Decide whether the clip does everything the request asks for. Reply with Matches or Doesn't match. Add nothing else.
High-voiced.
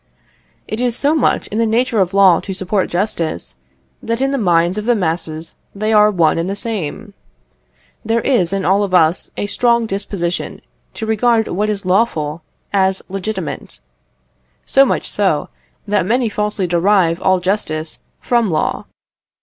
Matches